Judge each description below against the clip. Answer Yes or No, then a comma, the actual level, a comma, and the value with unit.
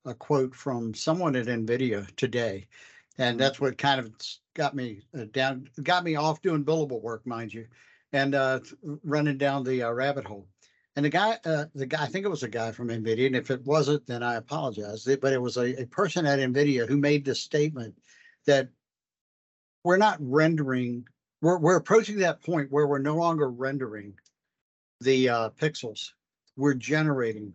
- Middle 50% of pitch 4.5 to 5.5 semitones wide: No, average, 3.8 semitones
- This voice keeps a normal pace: Yes, average, 180 wpm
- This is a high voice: No, low, 135 Hz